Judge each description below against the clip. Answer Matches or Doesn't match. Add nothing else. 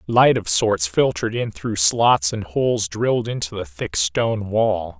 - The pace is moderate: Matches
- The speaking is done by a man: Matches